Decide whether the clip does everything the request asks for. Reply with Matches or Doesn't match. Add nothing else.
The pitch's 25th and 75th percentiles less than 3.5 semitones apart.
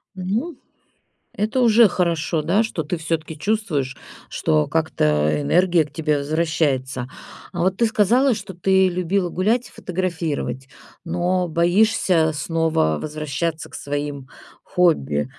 Doesn't match